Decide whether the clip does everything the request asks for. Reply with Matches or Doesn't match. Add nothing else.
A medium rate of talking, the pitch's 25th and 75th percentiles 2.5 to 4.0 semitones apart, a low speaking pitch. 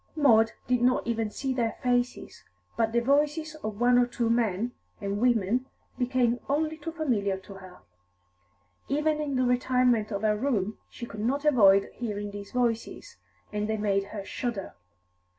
Doesn't match